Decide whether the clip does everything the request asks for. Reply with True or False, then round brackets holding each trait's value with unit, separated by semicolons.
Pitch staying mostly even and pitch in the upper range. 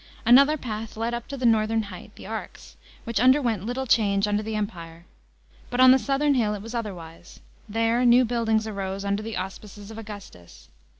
False (3.0 semitones; 220 Hz)